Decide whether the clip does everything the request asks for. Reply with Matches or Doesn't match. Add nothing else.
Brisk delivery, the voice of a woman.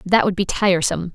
Matches